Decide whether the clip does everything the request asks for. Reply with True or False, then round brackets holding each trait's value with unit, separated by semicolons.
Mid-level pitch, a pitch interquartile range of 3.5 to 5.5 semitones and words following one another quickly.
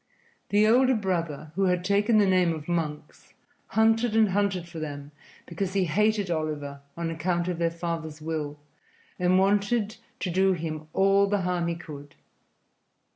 False (180 Hz; 3.8 semitones; 160 wpm)